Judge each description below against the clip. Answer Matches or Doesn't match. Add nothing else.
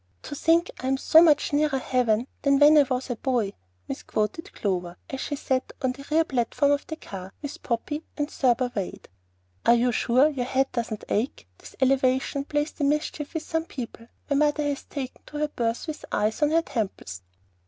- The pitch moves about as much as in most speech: Matches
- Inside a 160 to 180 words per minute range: Doesn't match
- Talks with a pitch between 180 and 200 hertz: Doesn't match